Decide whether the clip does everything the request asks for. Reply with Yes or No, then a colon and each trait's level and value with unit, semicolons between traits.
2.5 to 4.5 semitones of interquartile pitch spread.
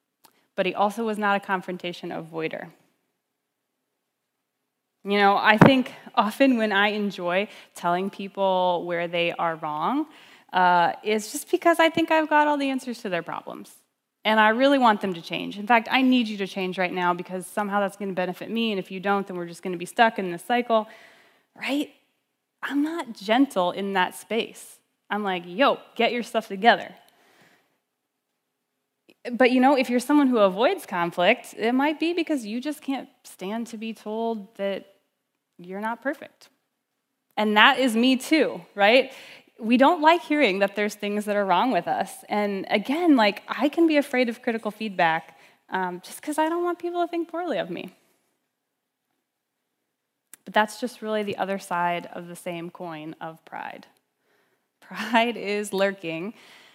No: wide, 5.4 semitones